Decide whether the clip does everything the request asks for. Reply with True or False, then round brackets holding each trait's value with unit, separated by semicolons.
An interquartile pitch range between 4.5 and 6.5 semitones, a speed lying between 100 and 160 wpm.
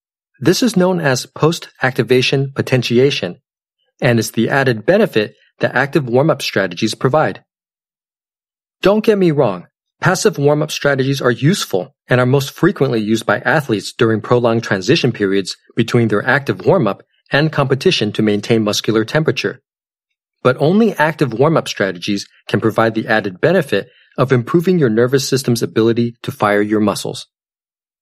True (4.8 semitones; 140 wpm)